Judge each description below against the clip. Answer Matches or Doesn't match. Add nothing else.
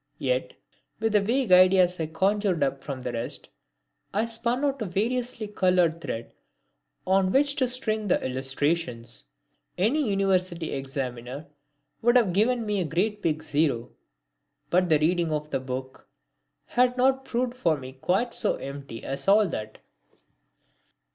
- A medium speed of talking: Matches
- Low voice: Doesn't match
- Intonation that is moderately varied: Doesn't match